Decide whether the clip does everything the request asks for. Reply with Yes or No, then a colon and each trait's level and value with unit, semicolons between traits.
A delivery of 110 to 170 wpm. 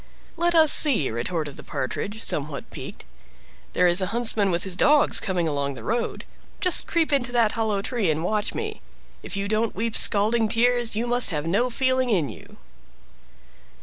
No: average, 180 wpm